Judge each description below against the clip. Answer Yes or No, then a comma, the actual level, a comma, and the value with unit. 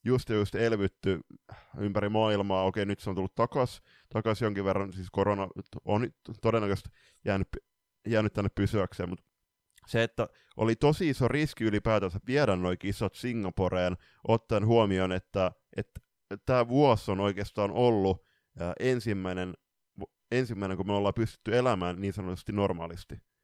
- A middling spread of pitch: Yes, average, 3.0 semitones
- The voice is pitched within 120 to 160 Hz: No, low, 100 Hz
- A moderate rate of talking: Yes, average, 140 wpm